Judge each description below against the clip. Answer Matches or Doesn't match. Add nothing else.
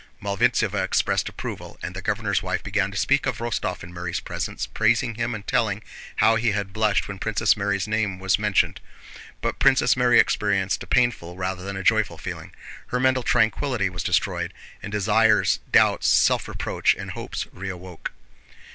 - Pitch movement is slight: Doesn't match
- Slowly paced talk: Doesn't match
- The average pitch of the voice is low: Matches